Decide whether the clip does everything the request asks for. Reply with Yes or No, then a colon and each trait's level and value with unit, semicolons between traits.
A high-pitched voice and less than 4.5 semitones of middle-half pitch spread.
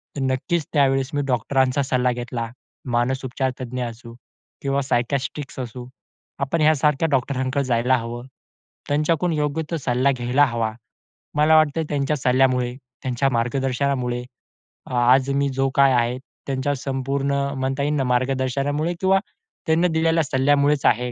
No: low, 135 Hz; narrow, 2.4 semitones